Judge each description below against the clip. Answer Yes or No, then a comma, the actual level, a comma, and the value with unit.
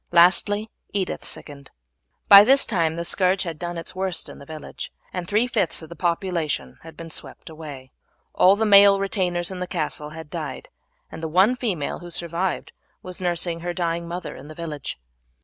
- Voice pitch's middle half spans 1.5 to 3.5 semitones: Yes, average, 2.8 semitones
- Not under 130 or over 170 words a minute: No, average, 185 wpm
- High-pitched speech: No, medium, 175 Hz